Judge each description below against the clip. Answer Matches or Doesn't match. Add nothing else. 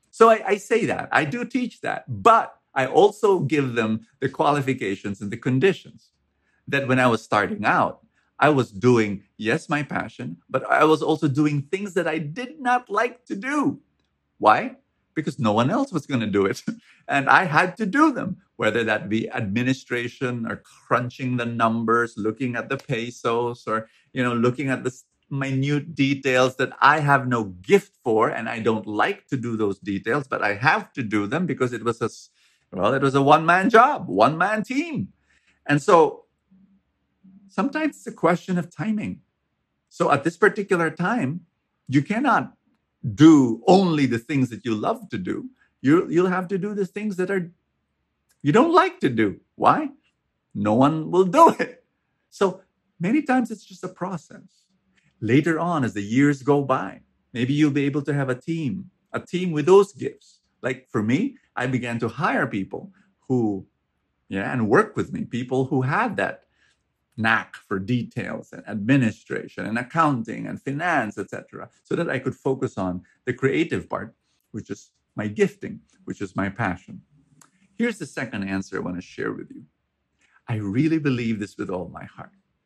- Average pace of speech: Matches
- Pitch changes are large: Matches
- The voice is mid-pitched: Matches